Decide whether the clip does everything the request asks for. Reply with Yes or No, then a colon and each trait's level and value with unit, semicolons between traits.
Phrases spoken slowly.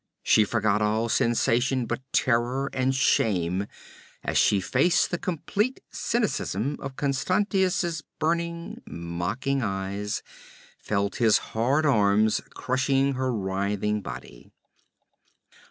Yes: slow, 105 wpm